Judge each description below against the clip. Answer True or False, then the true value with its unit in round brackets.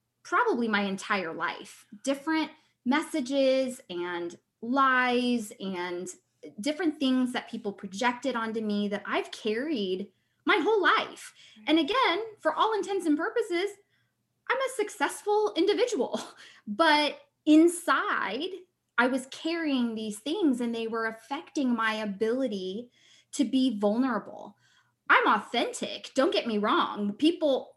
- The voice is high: True (265 Hz)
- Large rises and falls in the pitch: True (6.5 semitones)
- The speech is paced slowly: True (120 wpm)